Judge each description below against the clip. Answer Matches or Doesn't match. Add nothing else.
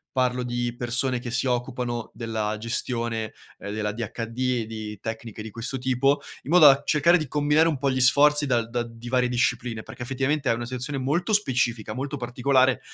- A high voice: Doesn't match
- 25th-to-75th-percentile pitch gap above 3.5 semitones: Doesn't match